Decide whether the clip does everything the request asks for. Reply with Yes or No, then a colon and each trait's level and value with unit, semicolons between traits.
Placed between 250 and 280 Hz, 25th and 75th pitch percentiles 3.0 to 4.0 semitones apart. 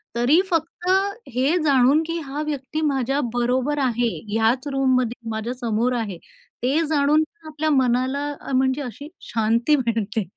Yes: very high, 260 Hz; average, 3.7 semitones